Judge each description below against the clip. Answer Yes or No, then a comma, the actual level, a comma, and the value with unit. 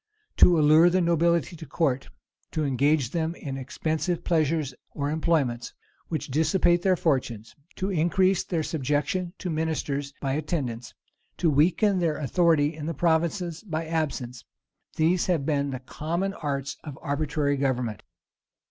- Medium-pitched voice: Yes, medium, 155 Hz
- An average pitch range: Yes, average, 3.3 semitones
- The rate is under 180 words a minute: Yes, average, 140 wpm